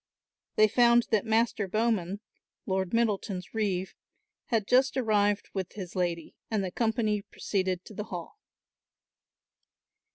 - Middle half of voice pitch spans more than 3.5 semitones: No, average, 3.1 semitones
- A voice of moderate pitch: No, high, 210 Hz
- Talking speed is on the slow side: Yes, slow, 125 wpm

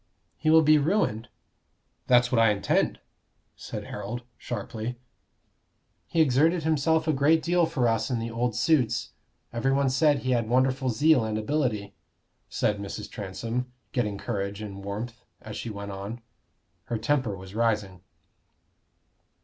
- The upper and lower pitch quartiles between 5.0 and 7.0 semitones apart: No, average, 4.6 semitones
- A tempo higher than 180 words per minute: No, average, 140 wpm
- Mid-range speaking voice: No, low, 120 Hz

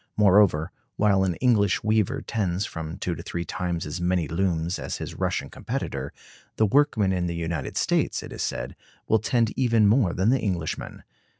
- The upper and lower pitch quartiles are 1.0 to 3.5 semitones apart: No, average, 4.1 semitones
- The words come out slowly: No, average, 180 wpm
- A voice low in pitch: Yes, very low, 95 Hz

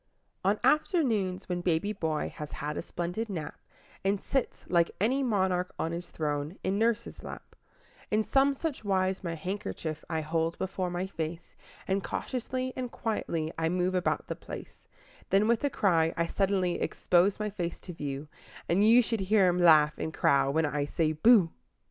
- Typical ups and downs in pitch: Yes, average, 4.5 semitones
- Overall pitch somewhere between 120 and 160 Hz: No, medium, 185 Hz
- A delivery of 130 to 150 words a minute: No, average, 175 wpm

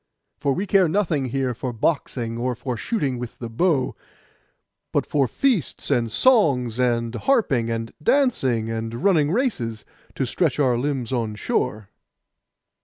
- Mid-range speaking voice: No, low, 130 Hz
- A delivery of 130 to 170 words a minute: Yes, average, 145 wpm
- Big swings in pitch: Yes, wide, 6.0 semitones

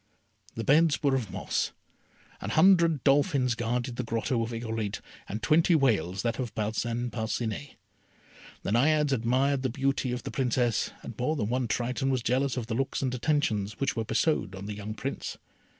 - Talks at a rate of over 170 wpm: Yes, average, 180 wpm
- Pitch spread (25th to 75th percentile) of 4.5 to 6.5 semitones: No, average, 3.4 semitones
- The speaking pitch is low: Yes, low, 125 Hz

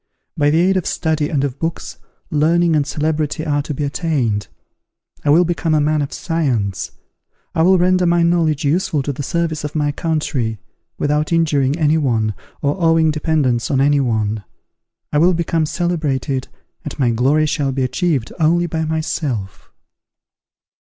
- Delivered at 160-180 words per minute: Yes, average, 165 wpm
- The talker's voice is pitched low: No, medium, 150 Hz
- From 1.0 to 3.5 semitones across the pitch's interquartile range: Yes, average, 2.9 semitones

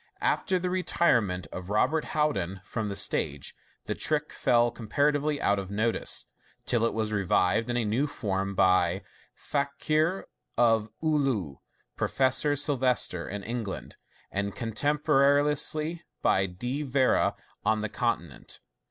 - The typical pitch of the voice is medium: No, low, 120 Hz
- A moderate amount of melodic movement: No, wide, 6.4 semitones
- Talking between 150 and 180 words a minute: No, slow, 135 wpm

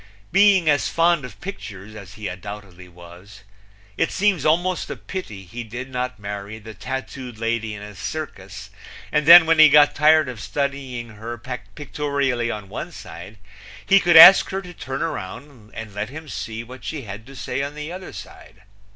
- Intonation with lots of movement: Yes, wide, 6.5 semitones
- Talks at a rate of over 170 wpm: Yes, average, 180 wpm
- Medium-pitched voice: No, low, 125 Hz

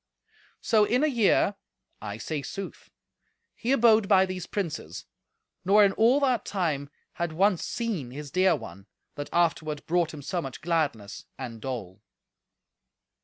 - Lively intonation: Yes, wide, 6.6 semitones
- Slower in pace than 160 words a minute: Yes, average, 145 wpm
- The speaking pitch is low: No, medium, 175 Hz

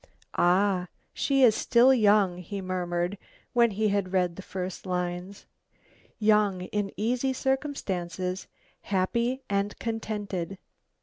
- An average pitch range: Yes, average, 3.4 semitones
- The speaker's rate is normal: No, slow, 115 wpm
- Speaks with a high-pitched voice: Yes, high, 200 Hz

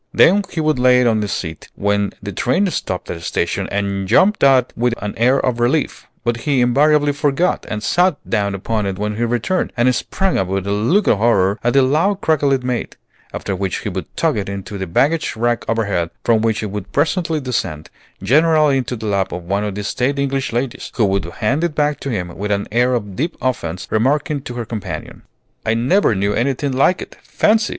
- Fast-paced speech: Yes, fast, 220 wpm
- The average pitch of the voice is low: Yes, low, 120 Hz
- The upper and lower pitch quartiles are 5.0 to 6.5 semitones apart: Yes, wide, 5.6 semitones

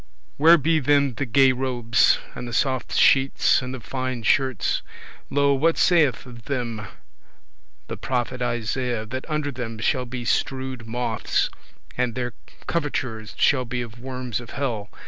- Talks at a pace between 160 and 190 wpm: No, average, 150 wpm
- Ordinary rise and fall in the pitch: No, narrow, 2.2 semitones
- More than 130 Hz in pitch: No, low, 125 Hz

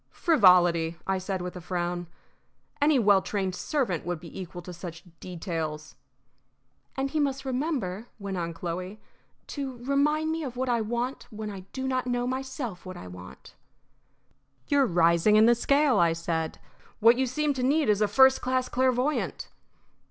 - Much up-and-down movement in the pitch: Yes, wide, 6.9 semitones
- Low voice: No, high, 215 Hz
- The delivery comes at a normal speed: Yes, average, 165 wpm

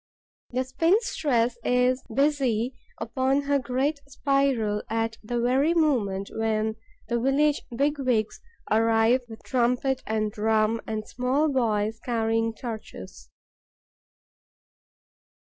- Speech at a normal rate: No, slow, 105 wpm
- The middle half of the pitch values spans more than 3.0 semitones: Yes, average, 3.5 semitones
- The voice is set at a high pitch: Yes, high, 240 Hz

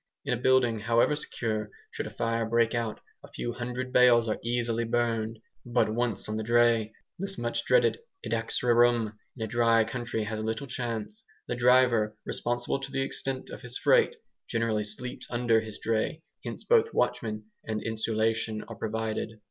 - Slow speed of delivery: No, average, 170 wpm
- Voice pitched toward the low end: Yes, low, 115 Hz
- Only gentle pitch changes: Yes, narrow, 1.9 semitones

